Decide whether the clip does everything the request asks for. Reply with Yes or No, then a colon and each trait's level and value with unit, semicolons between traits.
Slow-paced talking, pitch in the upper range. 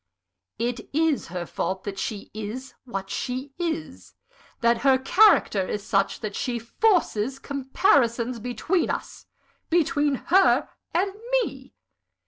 Yes: slow, 120 wpm; very high, 250 Hz